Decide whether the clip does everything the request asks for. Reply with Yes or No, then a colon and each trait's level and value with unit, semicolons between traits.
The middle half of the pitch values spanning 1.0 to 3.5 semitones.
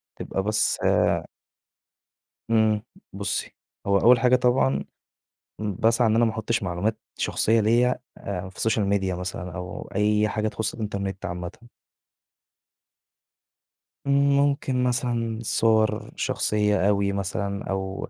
Yes: average, 2.9 semitones